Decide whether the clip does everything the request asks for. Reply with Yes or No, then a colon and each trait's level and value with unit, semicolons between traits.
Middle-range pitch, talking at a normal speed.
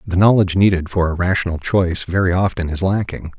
No: very low, 90 Hz; average, 195 wpm